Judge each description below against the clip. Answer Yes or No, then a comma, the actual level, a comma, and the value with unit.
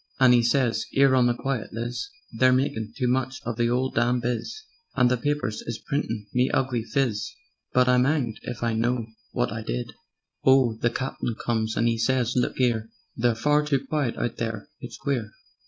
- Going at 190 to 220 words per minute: Yes, average, 195 wpm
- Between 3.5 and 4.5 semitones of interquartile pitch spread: No, narrow, 2.4 semitones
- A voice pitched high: No, low, 120 Hz